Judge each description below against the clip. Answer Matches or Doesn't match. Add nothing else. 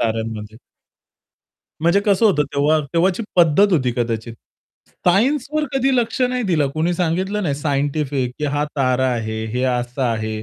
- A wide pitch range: Matches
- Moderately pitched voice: Matches